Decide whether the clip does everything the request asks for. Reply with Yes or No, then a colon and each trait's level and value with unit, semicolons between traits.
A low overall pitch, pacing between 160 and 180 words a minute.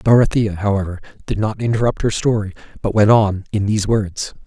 Yes: low, 105 Hz; average, 175 wpm